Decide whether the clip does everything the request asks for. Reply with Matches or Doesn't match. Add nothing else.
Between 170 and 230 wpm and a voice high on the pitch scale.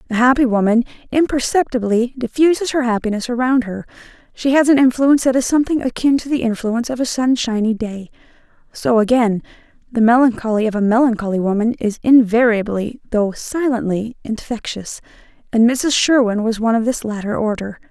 Doesn't match